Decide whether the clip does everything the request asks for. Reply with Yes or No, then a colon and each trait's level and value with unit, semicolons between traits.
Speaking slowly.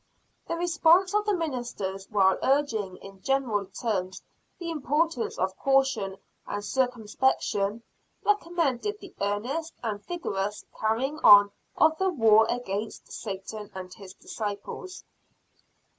Yes: slow, 115 wpm